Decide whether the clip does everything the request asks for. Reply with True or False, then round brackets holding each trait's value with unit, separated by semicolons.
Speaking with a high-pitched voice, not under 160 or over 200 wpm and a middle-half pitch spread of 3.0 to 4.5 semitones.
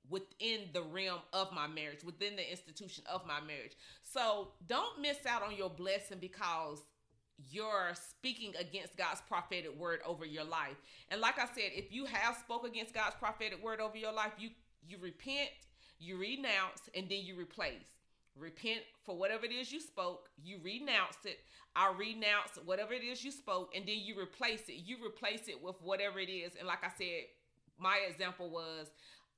True (195 Hz; 180 wpm; 4.2 semitones)